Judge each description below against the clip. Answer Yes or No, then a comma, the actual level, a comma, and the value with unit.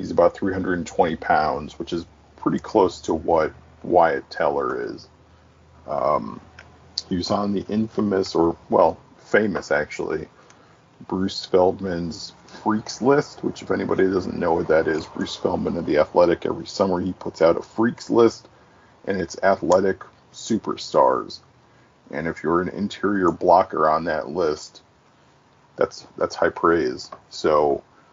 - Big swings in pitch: No, average, 3.5 semitones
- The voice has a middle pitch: No, very low, 95 Hz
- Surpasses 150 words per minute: No, average, 140 wpm